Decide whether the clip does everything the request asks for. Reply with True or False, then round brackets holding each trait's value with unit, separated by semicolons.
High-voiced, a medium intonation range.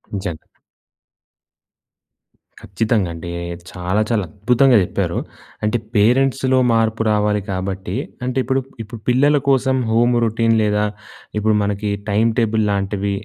False (110 Hz; 3.2 semitones)